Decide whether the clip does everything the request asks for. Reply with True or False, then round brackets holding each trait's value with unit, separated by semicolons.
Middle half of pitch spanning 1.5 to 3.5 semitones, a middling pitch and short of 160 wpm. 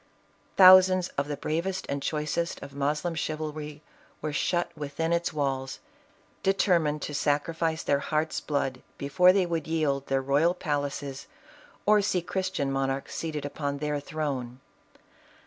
True (3.1 semitones; 150 Hz; 140 wpm)